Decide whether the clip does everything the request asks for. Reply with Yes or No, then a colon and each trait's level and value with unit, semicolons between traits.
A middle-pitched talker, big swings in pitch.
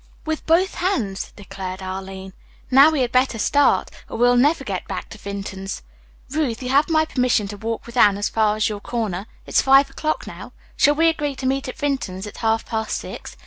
No: high, 240 Hz; wide, 5.9 semitones